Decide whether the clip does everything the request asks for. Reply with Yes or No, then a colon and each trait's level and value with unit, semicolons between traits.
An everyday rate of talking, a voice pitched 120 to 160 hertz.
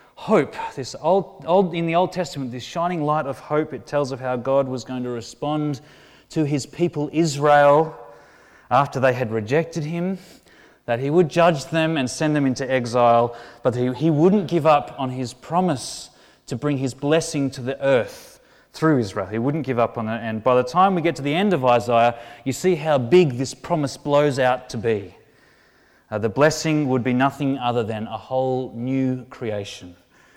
Yes: average, 195 wpm; low, 135 Hz